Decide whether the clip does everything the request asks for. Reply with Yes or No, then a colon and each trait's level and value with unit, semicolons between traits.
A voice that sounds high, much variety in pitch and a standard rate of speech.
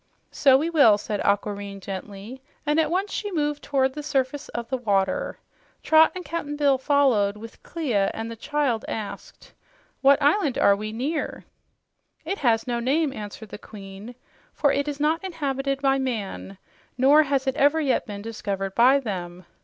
Yes: very high, 265 Hz; wide, 5.7 semitones; average, 170 wpm